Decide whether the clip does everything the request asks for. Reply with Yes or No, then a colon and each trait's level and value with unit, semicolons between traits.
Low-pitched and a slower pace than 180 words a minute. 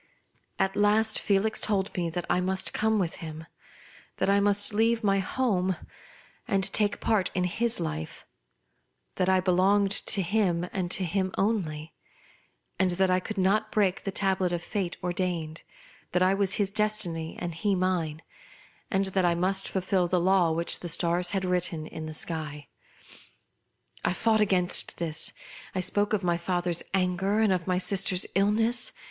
No: medium, 185 Hz; average, 170 wpm